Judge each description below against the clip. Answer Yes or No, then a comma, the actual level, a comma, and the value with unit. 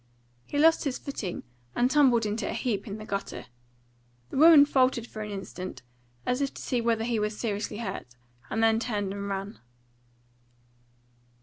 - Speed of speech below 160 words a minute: No, average, 165 wpm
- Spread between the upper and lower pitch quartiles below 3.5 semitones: No, average, 3.8 semitones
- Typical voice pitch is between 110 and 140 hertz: No, high, 225 Hz